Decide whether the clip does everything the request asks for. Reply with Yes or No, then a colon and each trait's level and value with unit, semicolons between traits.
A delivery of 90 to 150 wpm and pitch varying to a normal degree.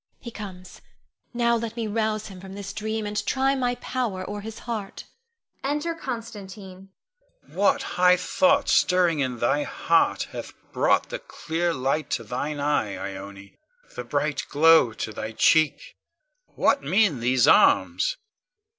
No: average, 145 wpm; wide, 7.5 semitones